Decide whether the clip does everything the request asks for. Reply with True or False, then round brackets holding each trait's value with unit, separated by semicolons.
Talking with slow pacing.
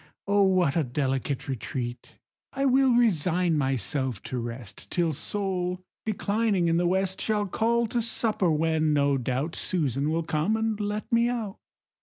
False (155 wpm)